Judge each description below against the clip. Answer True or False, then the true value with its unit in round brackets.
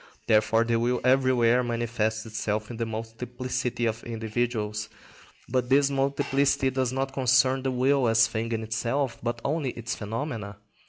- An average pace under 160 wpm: True (150 wpm)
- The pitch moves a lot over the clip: False (2.6 semitones)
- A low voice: True (120 Hz)